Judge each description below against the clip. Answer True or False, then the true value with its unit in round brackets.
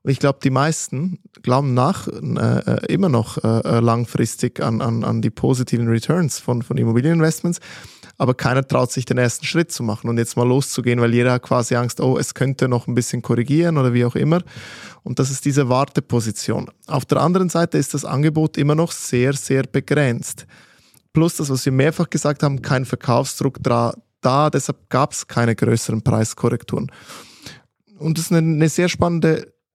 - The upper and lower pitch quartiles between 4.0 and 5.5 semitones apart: True (4.4 semitones)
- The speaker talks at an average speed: True (180 wpm)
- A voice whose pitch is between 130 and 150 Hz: True (135 Hz)